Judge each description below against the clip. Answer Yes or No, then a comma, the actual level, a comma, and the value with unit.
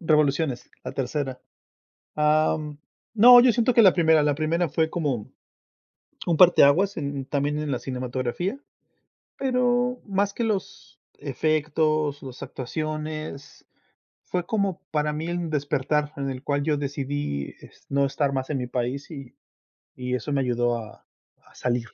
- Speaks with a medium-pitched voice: Yes, medium, 150 Hz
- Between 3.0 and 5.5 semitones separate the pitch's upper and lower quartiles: Yes, average, 3.6 semitones